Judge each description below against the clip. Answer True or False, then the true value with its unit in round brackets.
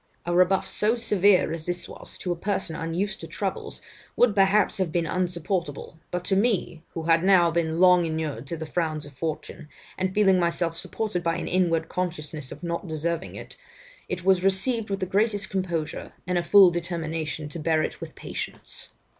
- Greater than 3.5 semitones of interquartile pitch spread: False (2.8 semitones)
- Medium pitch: True (175 Hz)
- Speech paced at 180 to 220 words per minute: True (190 wpm)